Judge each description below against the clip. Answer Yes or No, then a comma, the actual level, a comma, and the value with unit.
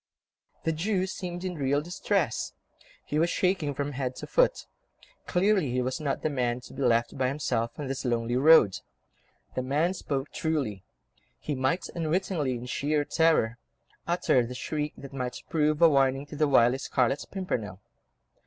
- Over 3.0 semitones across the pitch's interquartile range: Yes, average, 4.3 semitones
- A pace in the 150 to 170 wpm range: Yes, average, 165 wpm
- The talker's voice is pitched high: No, medium, 145 Hz